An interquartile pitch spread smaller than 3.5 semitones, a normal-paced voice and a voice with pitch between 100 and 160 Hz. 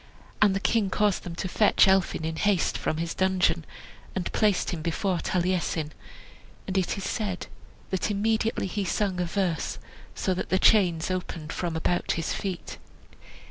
No: average, 2.7 semitones; average, 165 wpm; medium, 185 Hz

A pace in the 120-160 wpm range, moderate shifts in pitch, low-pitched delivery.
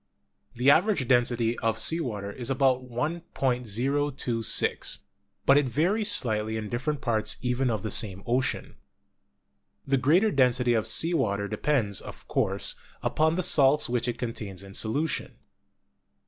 Yes: average, 140 wpm; average, 4.3 semitones; low, 125 Hz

